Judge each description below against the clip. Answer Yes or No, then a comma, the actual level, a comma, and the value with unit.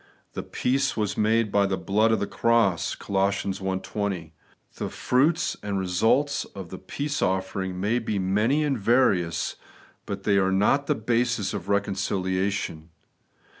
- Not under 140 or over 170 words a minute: Yes, average, 155 wpm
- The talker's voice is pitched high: No, low, 100 Hz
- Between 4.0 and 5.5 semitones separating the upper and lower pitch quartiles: No, average, 3.5 semitones